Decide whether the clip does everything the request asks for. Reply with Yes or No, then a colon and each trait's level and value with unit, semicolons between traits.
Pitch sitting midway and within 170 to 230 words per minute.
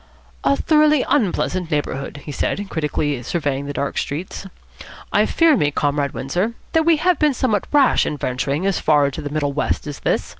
Yes: medium, 155 Hz; average, 185 wpm